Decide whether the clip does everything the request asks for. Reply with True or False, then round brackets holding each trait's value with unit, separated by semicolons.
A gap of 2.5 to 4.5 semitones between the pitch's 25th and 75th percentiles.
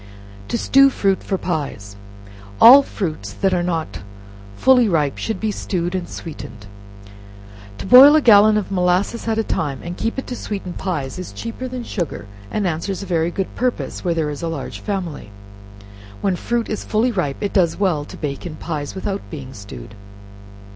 False (5.3 semitones)